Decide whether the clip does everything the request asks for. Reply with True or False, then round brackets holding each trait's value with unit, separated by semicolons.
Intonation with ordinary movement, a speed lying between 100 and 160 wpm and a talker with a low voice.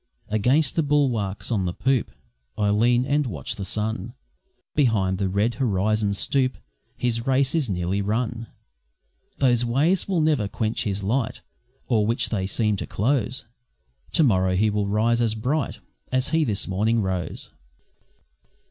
True (4.4 semitones; 150 wpm; 115 Hz)